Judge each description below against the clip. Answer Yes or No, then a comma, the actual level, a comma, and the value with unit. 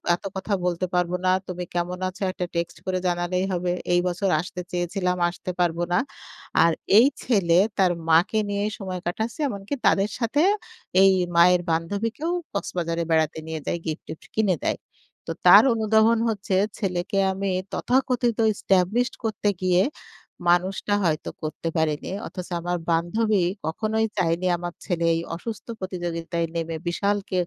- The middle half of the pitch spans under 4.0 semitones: Yes, average, 3.0 semitones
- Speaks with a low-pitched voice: No, medium, 180 Hz